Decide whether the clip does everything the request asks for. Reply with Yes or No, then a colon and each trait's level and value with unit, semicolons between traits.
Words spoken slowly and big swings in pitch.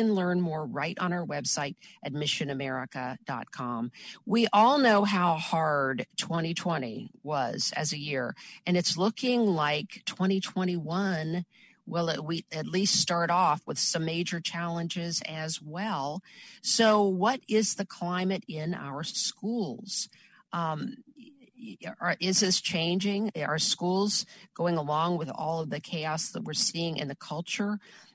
No: slow, 130 wpm; average, 4.6 semitones